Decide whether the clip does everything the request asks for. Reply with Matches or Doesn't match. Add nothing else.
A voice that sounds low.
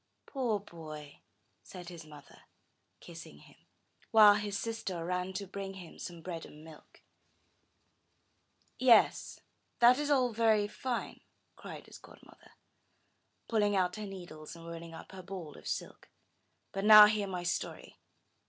Doesn't match